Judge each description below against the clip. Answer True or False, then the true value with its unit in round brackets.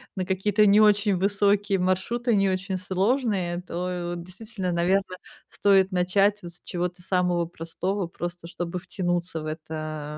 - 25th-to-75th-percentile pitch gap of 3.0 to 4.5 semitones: False (2.4 semitones)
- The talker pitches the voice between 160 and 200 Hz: True (185 Hz)